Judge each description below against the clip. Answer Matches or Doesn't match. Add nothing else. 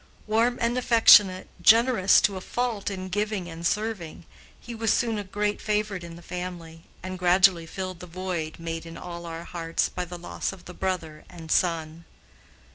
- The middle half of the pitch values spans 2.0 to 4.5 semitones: Matches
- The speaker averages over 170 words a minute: Matches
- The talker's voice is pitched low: Doesn't match